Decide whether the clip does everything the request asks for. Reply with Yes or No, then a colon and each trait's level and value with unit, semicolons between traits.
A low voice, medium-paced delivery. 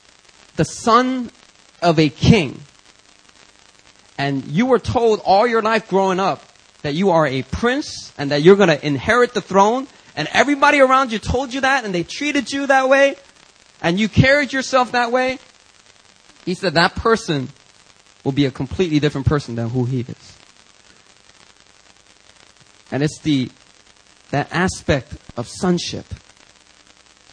No: medium, 150 Hz; average, 145 wpm